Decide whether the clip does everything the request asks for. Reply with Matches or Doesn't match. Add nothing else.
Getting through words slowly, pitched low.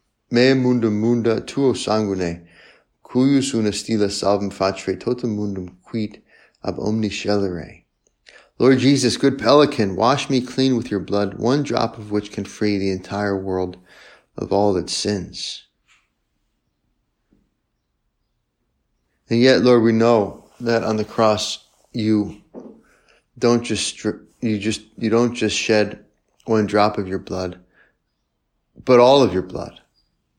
Matches